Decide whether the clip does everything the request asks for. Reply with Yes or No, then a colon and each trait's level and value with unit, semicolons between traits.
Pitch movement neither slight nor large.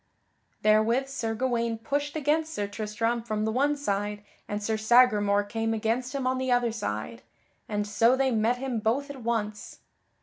Yes: average, 3.3 semitones